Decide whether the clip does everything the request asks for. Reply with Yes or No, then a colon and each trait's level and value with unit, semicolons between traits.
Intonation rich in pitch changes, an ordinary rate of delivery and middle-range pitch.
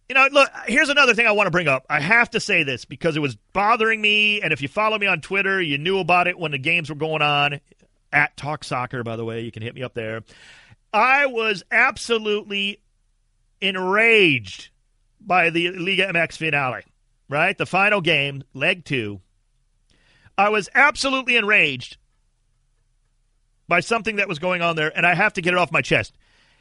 Yes: wide, 8.1 semitones; average, 190 wpm; medium, 165 Hz